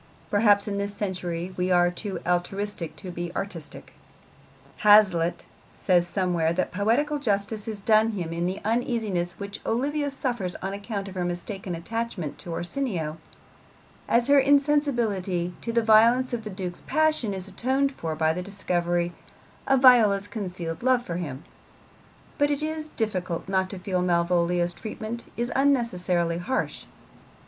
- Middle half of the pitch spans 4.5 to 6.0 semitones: Yes, average, 4.8 semitones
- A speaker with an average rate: Yes, average, 150 wpm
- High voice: Yes, high, 200 Hz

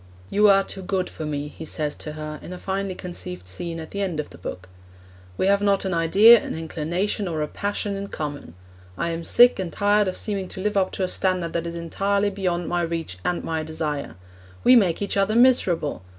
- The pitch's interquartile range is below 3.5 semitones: No, average, 3.8 semitones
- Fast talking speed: Yes, fast, 220 wpm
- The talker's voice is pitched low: No, medium, 180 Hz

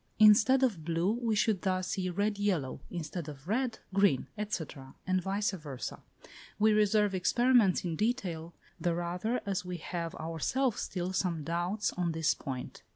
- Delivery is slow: No, average, 155 wpm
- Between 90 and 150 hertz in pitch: No, medium, 185 Hz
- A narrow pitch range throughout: No, average, 3.9 semitones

